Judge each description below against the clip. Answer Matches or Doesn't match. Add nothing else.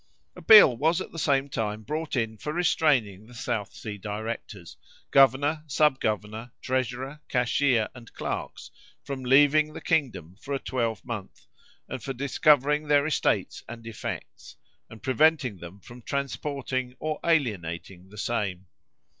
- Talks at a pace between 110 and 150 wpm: Matches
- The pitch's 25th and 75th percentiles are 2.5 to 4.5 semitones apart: Doesn't match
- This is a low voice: Matches